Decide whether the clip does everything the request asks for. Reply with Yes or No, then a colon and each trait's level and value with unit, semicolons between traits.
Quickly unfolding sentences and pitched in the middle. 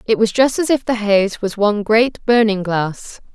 No: fast, 215 wpm; high, 215 Hz